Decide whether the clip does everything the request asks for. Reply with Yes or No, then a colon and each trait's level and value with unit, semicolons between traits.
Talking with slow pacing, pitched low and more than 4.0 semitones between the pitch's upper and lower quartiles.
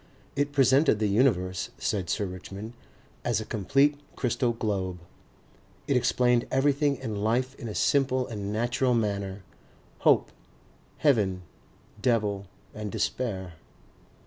Yes: slow, 120 wpm; low, 115 Hz; average, 4.5 semitones